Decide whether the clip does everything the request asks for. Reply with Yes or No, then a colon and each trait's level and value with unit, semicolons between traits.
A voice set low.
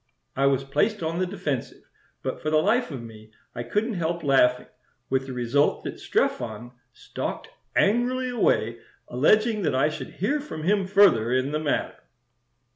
No: medium, 155 Hz